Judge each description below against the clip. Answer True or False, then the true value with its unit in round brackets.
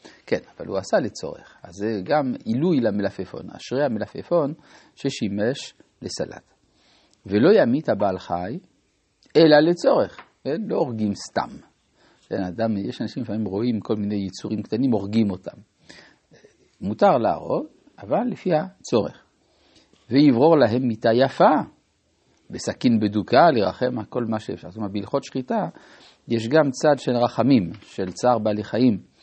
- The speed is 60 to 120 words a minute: False (130 wpm)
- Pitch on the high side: False (110 Hz)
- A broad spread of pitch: False (3.4 semitones)